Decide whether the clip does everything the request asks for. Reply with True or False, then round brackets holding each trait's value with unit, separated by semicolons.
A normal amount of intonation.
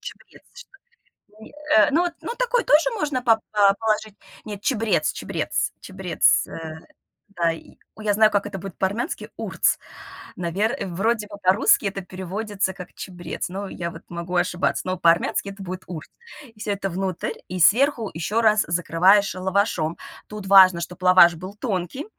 True (3.2 semitones)